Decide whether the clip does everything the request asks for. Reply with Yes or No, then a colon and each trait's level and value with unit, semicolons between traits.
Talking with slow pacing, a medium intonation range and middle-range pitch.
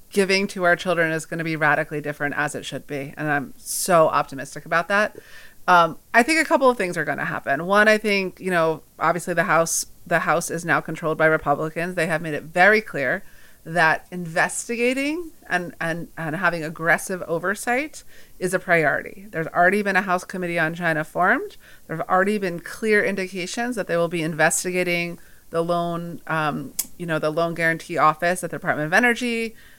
No: average, 195 wpm; average, 3.1 semitones; medium, 170 Hz